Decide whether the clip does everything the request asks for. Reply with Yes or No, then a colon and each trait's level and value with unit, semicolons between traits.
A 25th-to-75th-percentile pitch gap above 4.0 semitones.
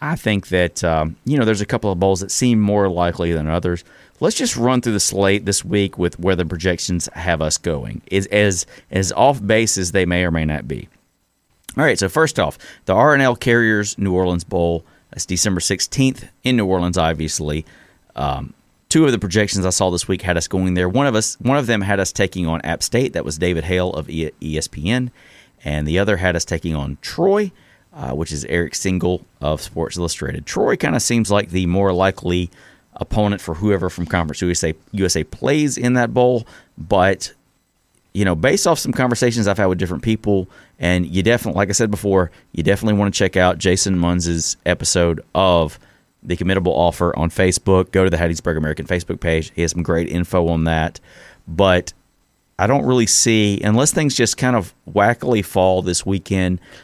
No: average, 3.6 semitones